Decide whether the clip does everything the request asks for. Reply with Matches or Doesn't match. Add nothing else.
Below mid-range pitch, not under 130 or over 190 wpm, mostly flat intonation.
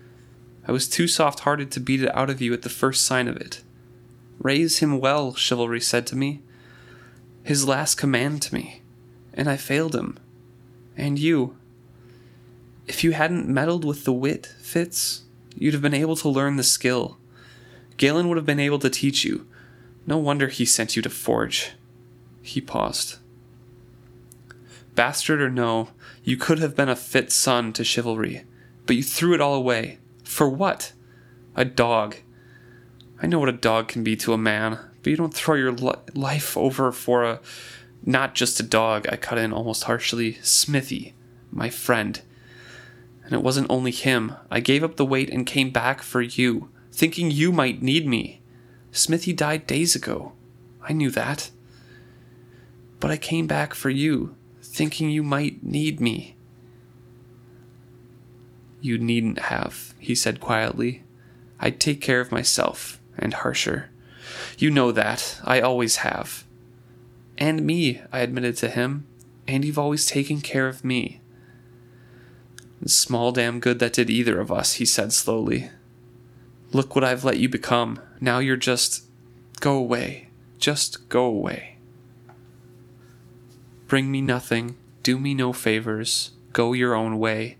Matches